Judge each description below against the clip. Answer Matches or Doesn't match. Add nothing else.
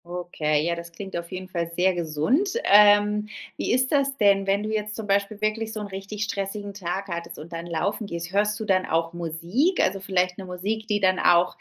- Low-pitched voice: Doesn't match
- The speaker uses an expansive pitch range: Doesn't match